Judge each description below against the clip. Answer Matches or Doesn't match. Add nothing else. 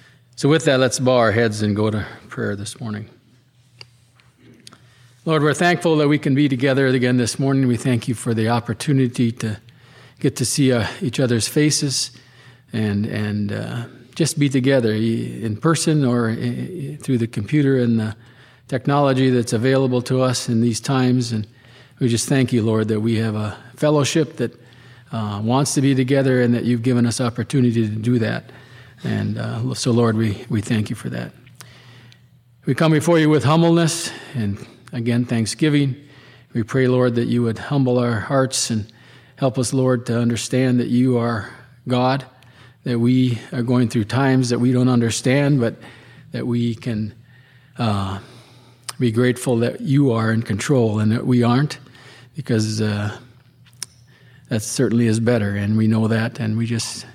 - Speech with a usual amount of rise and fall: Doesn't match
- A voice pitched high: Doesn't match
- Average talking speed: Matches